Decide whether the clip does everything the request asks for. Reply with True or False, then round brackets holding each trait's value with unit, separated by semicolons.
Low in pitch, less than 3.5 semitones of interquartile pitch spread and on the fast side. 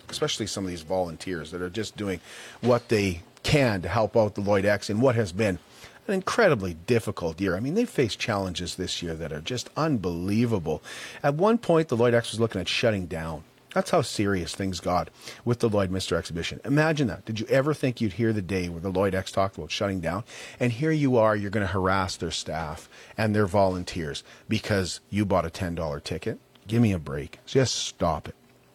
False (105 Hz; 4.6 semitones; 215 wpm)